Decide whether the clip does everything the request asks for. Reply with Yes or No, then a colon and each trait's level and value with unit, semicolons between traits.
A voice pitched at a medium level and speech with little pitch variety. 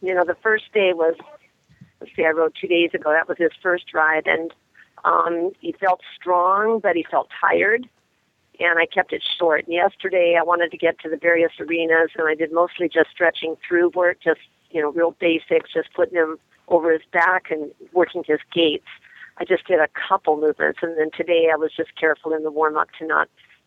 Yes: medium, 170 Hz; narrow, 1.9 semitones